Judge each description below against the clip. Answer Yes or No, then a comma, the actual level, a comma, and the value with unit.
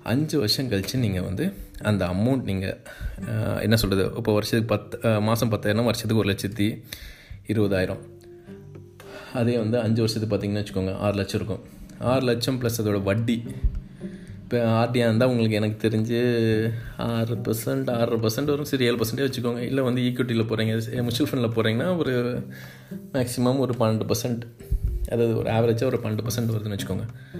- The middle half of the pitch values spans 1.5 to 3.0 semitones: Yes, average, 2.7 semitones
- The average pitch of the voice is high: No, low, 115 Hz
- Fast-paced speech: Yes, fast, 145 wpm